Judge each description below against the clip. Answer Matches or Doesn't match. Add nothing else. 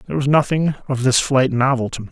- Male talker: Matches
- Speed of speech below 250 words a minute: Doesn't match